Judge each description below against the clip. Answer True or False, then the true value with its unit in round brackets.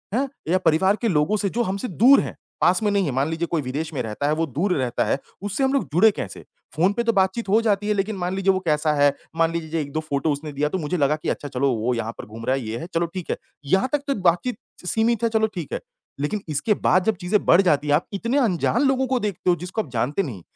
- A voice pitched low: False (175 Hz)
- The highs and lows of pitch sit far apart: True (6.0 semitones)